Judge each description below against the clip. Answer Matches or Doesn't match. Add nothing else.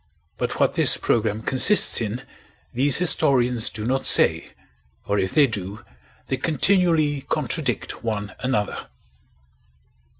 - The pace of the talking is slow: Matches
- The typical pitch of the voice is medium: Doesn't match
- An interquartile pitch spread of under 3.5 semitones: Doesn't match